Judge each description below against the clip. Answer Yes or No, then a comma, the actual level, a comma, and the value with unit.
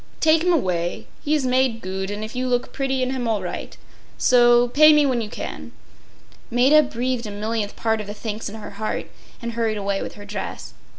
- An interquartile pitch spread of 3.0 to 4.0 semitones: Yes, average, 3.7 semitones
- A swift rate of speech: Yes, fast, 215 wpm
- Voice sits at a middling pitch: No, high, 230 Hz